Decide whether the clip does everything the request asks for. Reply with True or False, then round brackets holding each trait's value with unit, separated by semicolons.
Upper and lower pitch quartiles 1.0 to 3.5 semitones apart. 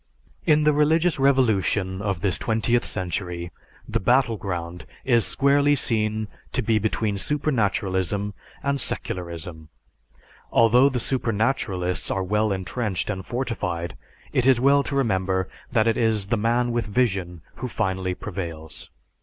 False (4.9 semitones)